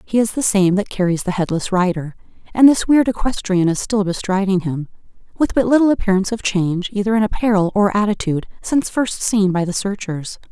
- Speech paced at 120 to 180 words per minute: No, average, 195 wpm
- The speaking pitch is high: Yes, high, 200 Hz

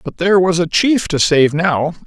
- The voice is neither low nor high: Yes, medium, 170 Hz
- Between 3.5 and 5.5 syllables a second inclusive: Yes, 4.9 syllables/s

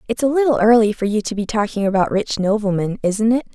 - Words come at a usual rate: No, fast, 235 wpm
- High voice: Yes, high, 215 Hz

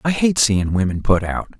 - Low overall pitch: Yes, low, 115 Hz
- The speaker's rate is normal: No, fast, 225 wpm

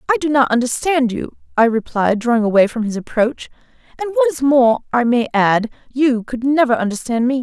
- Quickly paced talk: No, average, 195 wpm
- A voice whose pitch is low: No, very high, 250 Hz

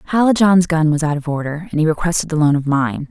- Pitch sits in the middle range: Yes, medium, 160 Hz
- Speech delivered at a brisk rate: Yes, fast, 250 wpm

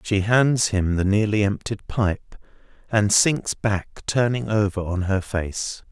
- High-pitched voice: No, low, 105 Hz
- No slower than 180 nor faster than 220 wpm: No, average, 150 wpm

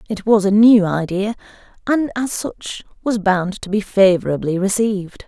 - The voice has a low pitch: No, high, 205 Hz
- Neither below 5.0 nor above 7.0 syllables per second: No, 4.6 syllables/s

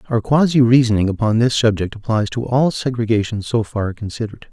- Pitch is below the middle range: Yes, low, 115 Hz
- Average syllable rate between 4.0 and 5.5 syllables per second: No, 5.7 syllables/s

